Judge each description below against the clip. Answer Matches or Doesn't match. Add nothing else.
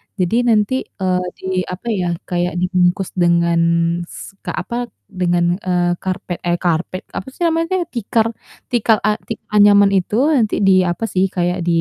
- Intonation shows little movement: Doesn't match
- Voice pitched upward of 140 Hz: Matches